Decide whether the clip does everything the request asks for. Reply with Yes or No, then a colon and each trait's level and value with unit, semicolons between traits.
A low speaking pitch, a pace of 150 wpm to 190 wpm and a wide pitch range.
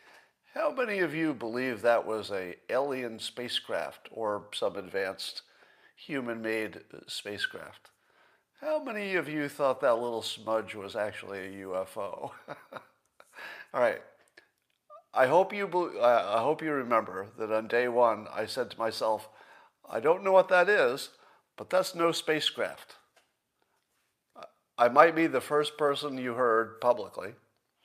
No: low, 130 Hz; average, 140 wpm; wide, 7.3 semitones